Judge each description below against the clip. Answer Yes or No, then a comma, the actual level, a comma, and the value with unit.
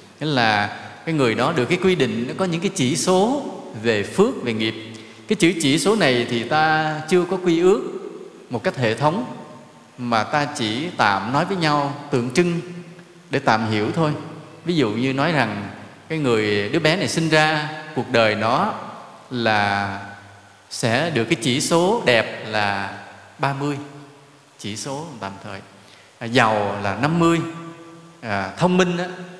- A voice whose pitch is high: No, medium, 140 Hz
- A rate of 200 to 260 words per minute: No, average, 170 wpm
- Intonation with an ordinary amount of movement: No, wide, 7.1 semitones